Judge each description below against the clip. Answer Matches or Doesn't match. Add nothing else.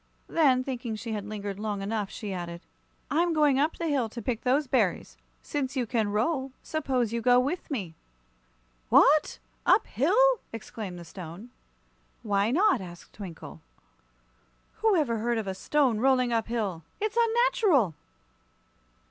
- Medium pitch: Doesn't match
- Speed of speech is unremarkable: Matches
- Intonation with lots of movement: Matches